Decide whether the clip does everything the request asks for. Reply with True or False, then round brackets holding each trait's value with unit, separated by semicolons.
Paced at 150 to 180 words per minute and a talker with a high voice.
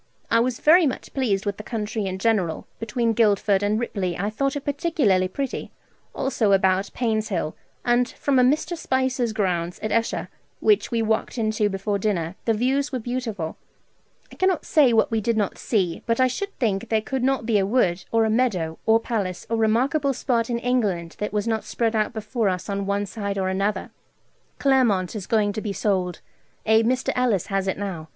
False (195 wpm; 220 Hz)